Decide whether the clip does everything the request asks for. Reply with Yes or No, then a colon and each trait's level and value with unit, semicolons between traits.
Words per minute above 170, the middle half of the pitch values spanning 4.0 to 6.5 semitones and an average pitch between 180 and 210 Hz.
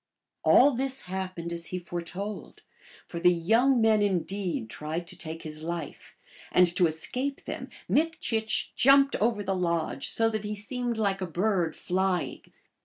No: average, 160 wpm; average, 4.7 semitones; high, 190 Hz